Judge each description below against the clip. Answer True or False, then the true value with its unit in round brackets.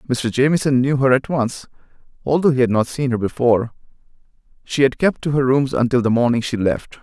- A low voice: True (130 Hz)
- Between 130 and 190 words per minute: False (205 wpm)